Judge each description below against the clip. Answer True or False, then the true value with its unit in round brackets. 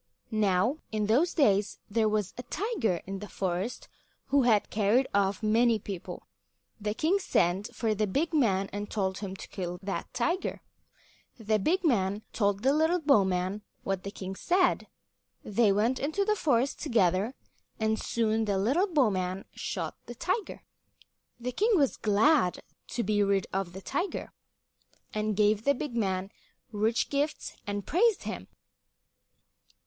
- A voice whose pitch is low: False (215 Hz)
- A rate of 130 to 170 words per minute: True (155 wpm)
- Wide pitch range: True (5.8 semitones)